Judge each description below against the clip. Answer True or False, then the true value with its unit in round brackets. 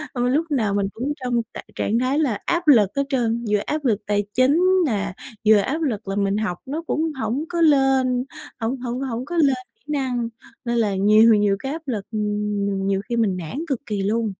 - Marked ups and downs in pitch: False (4.6 semitones)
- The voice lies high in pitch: True (235 Hz)